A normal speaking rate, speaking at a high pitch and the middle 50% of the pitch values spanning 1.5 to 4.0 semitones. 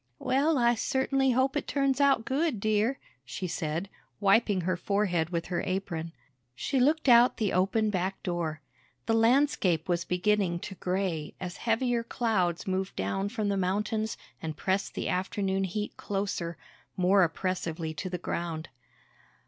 No: average, 150 wpm; high, 195 Hz; average, 4.7 semitones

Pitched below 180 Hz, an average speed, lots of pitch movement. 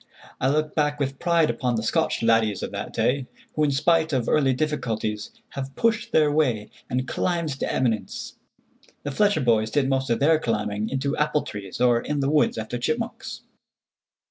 No: low, 135 Hz; average, 180 wpm; average, 4.6 semitones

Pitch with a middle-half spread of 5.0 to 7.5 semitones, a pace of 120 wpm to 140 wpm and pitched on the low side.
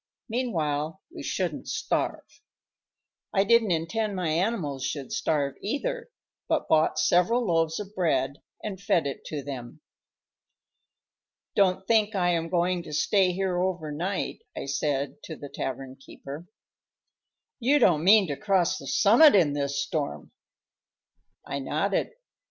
No: wide, 5.4 semitones; slow, 135 wpm; medium, 175 Hz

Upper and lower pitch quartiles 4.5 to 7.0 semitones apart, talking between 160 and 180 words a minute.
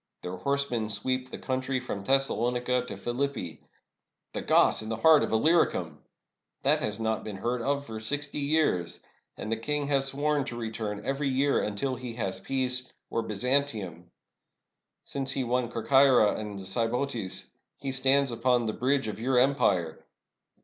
No: average, 4.0 semitones; average, 170 wpm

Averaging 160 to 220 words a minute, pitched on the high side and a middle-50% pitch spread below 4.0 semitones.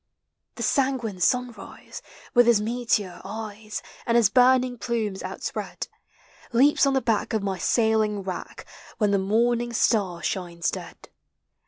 No: slow, 135 wpm; high, 220 Hz; average, 3.3 semitones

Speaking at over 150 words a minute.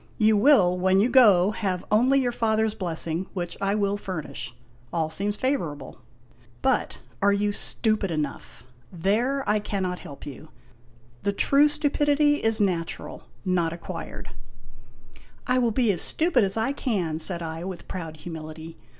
Yes: average, 160 wpm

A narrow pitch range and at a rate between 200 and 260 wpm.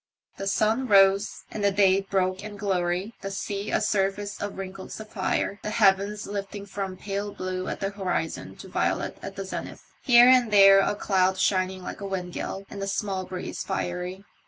No: narrow, 1.5 semitones; average, 185 wpm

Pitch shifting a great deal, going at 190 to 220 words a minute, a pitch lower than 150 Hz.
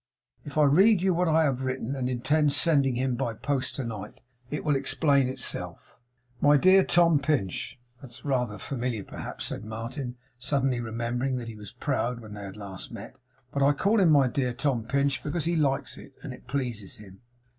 No: average, 3.5 semitones; average, 200 wpm; low, 135 Hz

